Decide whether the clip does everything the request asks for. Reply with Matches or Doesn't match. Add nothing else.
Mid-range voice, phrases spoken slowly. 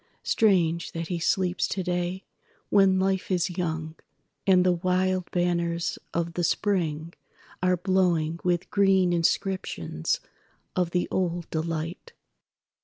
Matches